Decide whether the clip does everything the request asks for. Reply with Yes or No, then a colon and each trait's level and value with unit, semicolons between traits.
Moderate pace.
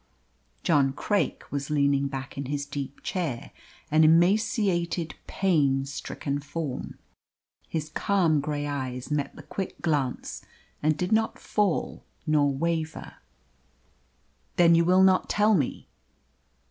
No: slow, 120 wpm